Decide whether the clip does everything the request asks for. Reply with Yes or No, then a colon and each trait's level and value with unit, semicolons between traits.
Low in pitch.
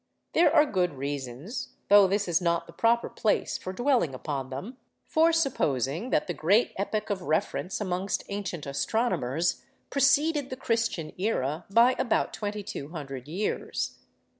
No: high, 190 Hz